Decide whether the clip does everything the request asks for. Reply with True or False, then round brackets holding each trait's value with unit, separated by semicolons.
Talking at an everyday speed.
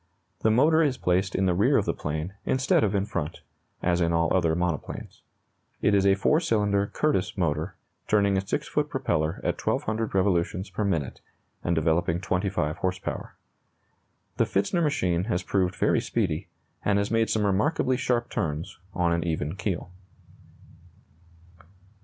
True (160 wpm)